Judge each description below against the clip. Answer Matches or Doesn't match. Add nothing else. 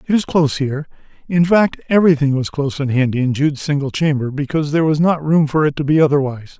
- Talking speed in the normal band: Doesn't match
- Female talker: Doesn't match